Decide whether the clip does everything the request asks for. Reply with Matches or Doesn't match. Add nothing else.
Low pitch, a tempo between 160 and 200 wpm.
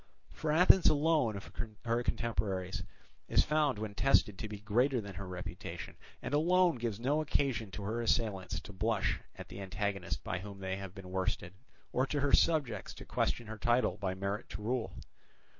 Matches